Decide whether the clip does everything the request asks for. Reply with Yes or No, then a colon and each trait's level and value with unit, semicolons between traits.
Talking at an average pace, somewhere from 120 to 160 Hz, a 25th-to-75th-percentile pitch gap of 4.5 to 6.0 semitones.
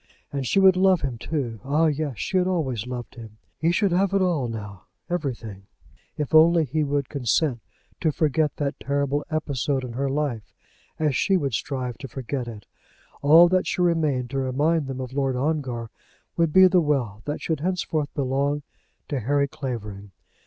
No: average, 180 wpm; medium, 140 Hz; average, 4.1 semitones